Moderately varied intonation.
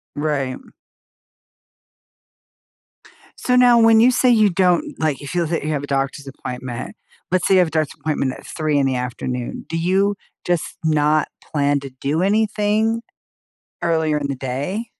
No: wide, 6.0 semitones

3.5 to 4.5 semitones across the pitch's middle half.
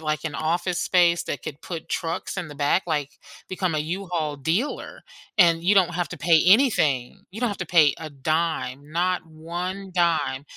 No: average, 2.9 semitones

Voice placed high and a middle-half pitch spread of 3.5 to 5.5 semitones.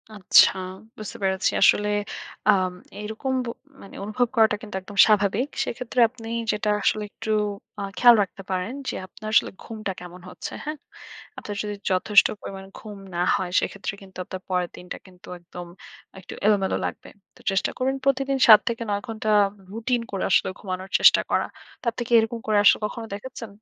No: high, 210 Hz; average, 3.1 semitones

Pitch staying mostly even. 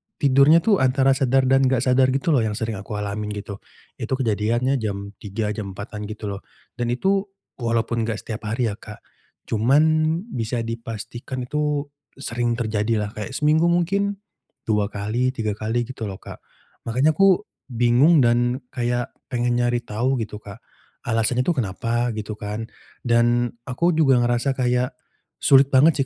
No: average, 3.5 semitones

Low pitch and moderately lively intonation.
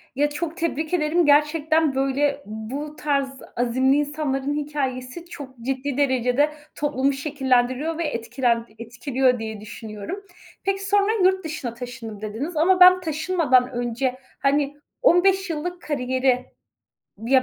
No: very high, 280 Hz; average, 3.8 semitones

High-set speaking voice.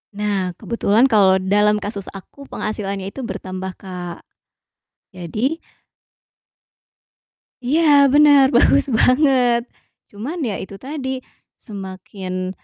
Yes: high, 210 Hz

